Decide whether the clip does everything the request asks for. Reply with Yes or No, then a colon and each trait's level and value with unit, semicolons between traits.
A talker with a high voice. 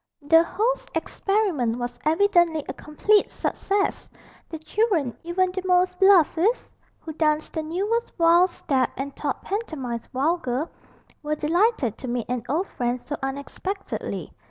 Yes: very high, 325 Hz